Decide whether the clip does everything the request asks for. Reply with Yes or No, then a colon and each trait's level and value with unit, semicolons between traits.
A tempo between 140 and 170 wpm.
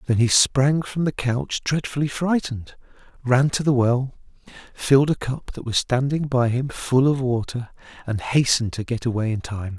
No: average, 185 wpm